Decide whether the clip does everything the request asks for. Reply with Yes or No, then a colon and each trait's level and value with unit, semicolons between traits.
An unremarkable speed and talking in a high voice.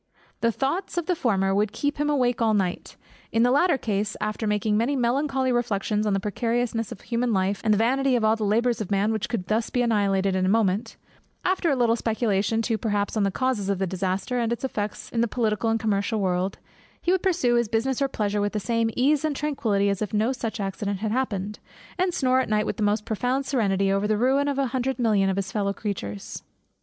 No: fast, 235 wpm; high, 225 Hz